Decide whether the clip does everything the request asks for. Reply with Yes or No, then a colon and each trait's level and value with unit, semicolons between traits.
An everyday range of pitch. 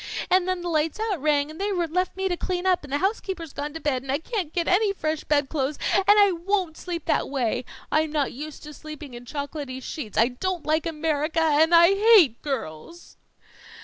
Yes: average, 4.0 semitones